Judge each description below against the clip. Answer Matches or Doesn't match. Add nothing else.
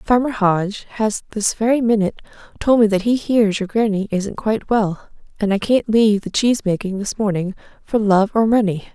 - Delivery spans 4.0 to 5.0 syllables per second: Doesn't match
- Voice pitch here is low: Doesn't match